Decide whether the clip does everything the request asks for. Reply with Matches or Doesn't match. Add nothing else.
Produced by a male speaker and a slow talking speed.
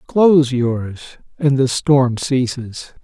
Matches